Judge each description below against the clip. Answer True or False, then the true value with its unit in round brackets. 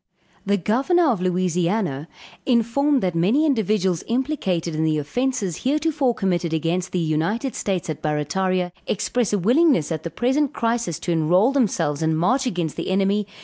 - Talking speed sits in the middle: True (160 wpm)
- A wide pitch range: True (6.7 semitones)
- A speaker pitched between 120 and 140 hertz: False (190 Hz)